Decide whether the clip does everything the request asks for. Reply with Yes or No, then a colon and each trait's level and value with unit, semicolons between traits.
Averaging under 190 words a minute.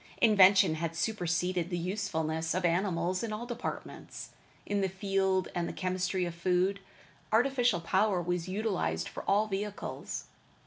Yes: average, 140 wpm